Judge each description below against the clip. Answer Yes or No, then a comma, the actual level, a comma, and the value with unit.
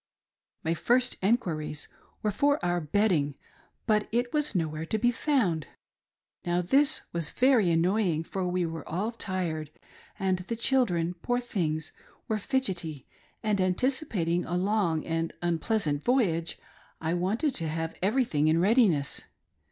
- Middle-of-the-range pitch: Yes, medium, 180 Hz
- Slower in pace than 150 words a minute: Yes, average, 140 wpm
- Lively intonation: Yes, wide, 5.8 semitones